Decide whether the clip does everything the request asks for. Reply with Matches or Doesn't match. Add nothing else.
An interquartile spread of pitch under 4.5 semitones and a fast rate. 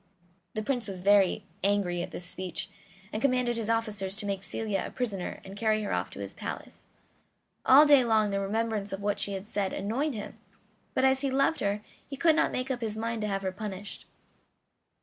Matches